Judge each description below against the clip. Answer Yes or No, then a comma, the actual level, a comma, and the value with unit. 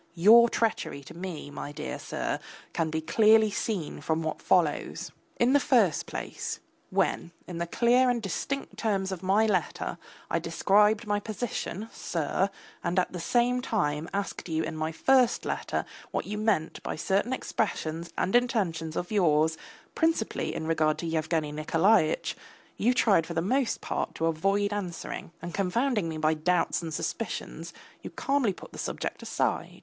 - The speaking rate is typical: Yes, average, 165 wpm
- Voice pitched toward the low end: No, high, 190 Hz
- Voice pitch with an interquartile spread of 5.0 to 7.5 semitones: Yes, wide, 5.5 semitones